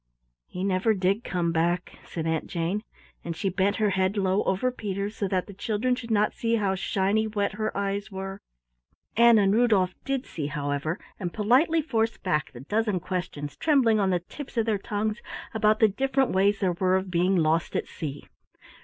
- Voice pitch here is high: Yes, high, 200 Hz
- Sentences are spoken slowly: No, average, 190 wpm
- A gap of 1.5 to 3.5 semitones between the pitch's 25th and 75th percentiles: Yes, average, 3.2 semitones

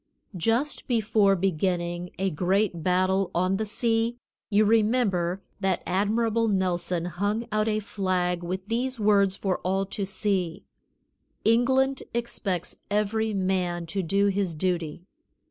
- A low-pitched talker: No, high, 195 Hz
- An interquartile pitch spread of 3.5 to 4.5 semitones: No, average, 3.1 semitones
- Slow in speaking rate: Yes, slow, 130 wpm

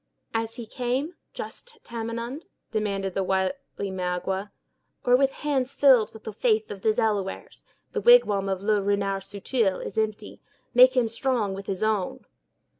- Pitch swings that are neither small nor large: Yes, average, 3.9 semitones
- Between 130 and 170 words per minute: Yes, average, 155 wpm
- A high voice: Yes, high, 215 Hz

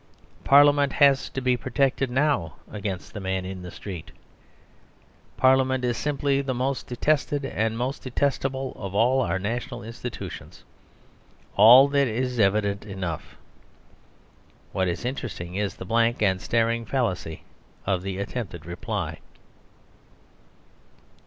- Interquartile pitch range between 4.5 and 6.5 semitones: Yes, wide, 5.4 semitones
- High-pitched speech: No, low, 120 Hz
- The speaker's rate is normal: No, slow, 125 wpm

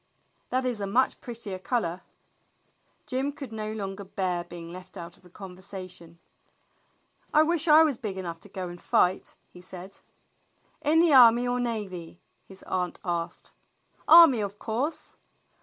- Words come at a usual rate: Yes, average, 155 wpm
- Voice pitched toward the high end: Yes, high, 200 Hz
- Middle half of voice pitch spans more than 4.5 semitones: Yes, wide, 5.6 semitones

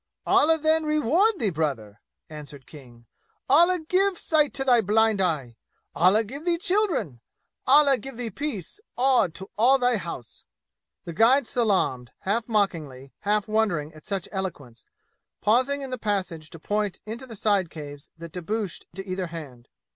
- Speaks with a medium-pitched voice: No, high, 210 Hz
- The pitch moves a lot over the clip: Yes, wide, 8.5 semitones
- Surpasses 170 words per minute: No, average, 155 wpm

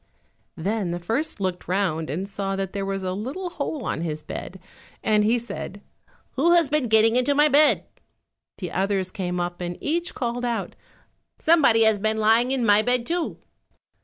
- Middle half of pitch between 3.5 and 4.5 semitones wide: No, average, 5.2 semitones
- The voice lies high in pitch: Yes, high, 215 Hz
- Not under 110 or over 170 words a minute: No, average, 180 wpm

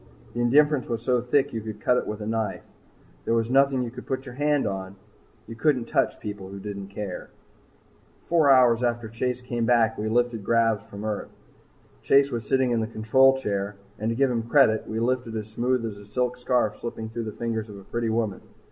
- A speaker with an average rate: No, fast, 220 wpm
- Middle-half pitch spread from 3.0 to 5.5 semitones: No, narrow, 2.6 semitones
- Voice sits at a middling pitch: No, low, 115 Hz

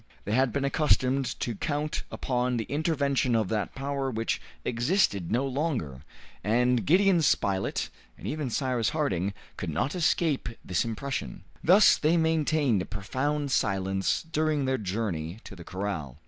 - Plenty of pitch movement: Yes, wide, 6.4 semitones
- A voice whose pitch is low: Yes, low, 130 Hz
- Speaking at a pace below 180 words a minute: Yes, average, 145 wpm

